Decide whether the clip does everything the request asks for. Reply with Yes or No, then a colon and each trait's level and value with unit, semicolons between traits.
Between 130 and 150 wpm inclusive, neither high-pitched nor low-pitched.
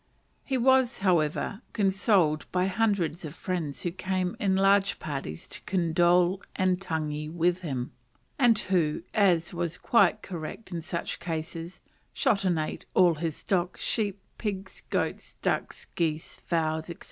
Yes: average, 145 wpm; medium, 180 Hz